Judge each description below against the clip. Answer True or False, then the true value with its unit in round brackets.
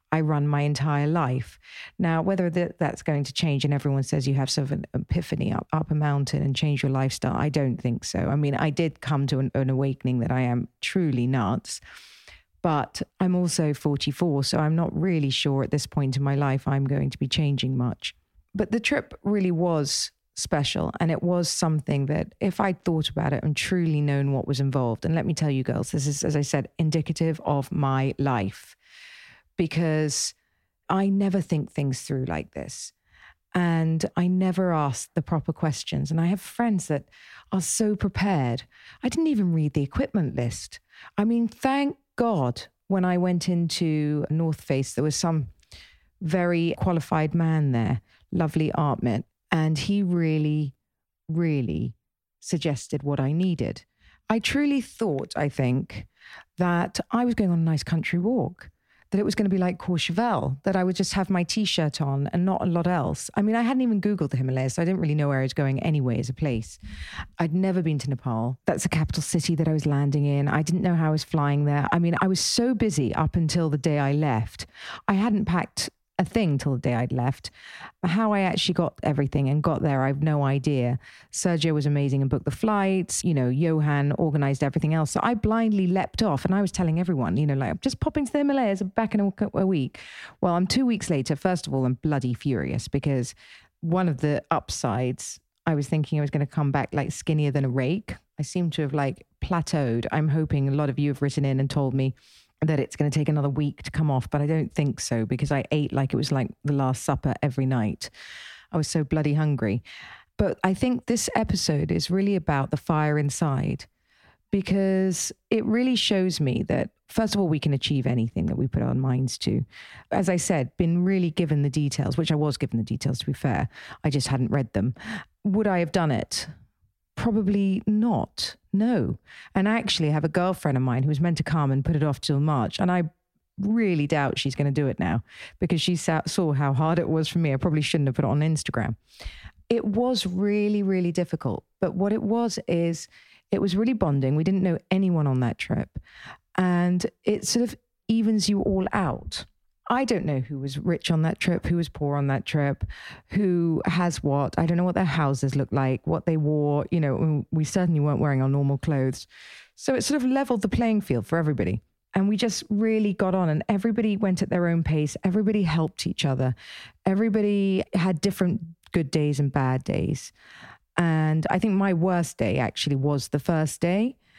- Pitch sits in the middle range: True (155 Hz)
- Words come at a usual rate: False (210 wpm)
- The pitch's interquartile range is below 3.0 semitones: False (4.8 semitones)